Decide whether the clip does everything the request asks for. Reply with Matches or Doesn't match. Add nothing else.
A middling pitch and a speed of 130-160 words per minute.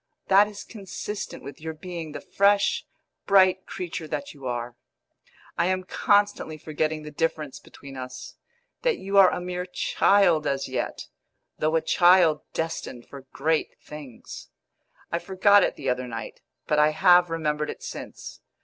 Matches